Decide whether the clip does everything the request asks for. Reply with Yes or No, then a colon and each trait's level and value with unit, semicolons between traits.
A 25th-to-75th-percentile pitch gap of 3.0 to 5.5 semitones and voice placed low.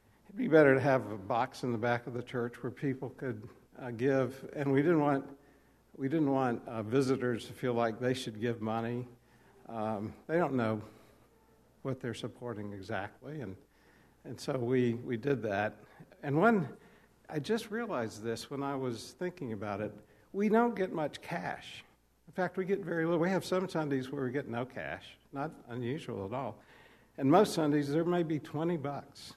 Yes: average, 4.6 semitones; low, 130 Hz